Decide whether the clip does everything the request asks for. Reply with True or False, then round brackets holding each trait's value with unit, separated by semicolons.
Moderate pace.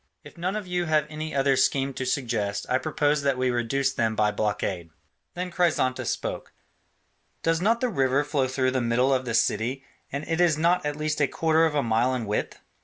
False (210 wpm)